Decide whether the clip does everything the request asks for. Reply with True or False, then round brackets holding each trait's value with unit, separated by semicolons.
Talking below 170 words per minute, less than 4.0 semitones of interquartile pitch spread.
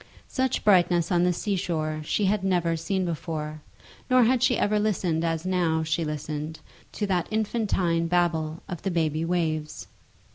True (160 wpm; 3.2 semitones)